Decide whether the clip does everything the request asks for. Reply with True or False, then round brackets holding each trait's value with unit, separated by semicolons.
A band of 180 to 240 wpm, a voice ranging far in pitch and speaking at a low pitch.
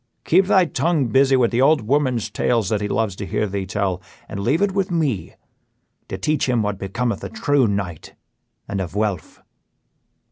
True (185 wpm; 6.3 semitones; 115 Hz)